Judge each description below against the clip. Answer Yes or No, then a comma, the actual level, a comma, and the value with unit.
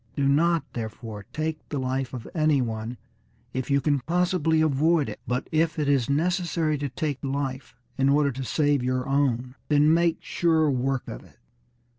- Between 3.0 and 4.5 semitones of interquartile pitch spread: Yes, average, 3.4 semitones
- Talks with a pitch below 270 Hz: Yes, medium, 140 Hz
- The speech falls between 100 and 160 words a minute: No, average, 175 wpm